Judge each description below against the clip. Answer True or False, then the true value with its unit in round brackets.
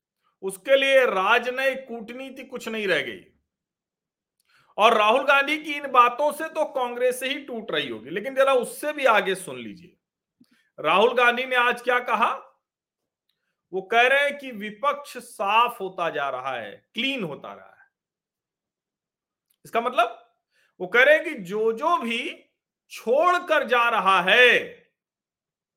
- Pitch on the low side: False (250 Hz)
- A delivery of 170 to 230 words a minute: False (150 wpm)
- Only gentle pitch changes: False (3.8 semitones)